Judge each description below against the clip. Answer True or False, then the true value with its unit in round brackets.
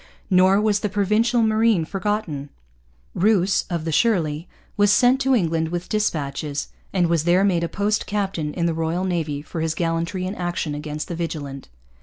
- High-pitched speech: False (175 Hz)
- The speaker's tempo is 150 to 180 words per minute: True (175 wpm)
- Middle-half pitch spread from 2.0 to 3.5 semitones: False (4.2 semitones)